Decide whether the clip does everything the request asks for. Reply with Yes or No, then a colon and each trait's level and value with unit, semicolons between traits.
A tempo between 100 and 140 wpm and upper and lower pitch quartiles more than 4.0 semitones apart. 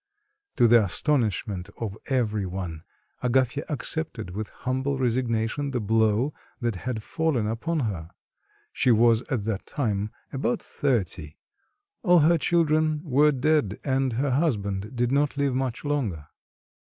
Yes: slow, 135 wpm; average, 5.0 semitones